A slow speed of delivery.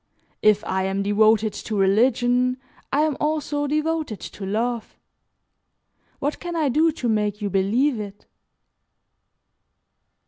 Yes: slow, 125 wpm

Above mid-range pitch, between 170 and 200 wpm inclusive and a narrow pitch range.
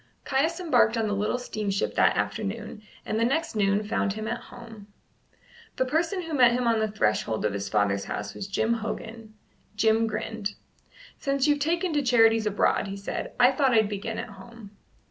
No: high, 225 Hz; average, 185 wpm; average, 3.5 semitones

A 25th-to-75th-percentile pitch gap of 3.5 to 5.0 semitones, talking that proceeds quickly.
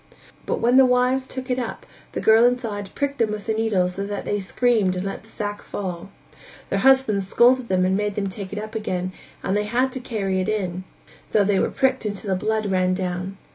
Yes: average, 4.0 semitones; fast, 225 wpm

